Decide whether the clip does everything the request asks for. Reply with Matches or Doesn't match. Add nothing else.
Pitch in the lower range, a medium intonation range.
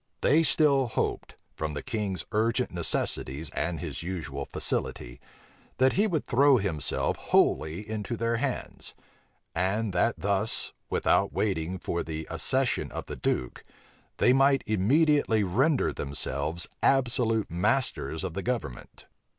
Doesn't match